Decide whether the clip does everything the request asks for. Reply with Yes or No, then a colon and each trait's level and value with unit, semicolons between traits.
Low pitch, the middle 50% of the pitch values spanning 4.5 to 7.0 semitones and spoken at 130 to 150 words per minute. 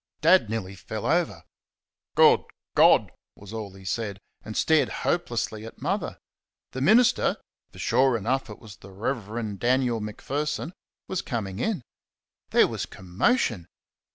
Yes: low, 115 Hz; average, 4.8 semitones; slow, 135 wpm